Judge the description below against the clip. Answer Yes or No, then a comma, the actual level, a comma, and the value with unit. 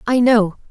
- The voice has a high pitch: Yes, high, 225 Hz